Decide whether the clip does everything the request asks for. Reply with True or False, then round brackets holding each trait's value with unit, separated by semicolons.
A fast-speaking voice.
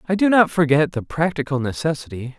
False (175 wpm)